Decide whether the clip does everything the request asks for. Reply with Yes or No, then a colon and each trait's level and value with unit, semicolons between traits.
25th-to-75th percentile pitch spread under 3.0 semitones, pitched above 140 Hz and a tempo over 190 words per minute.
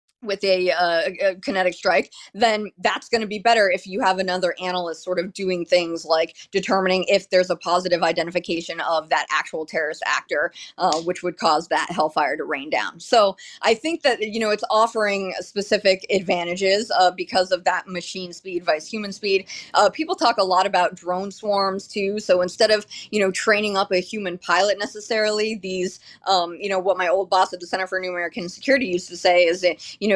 Yes: narrow, 2.6 semitones; high, 190 Hz; fast, 205 wpm